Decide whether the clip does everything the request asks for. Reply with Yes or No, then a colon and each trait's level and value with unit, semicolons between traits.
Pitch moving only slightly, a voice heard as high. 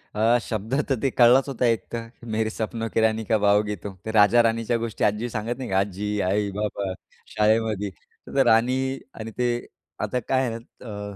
No: narrow, 2.2 semitones; low, 110 Hz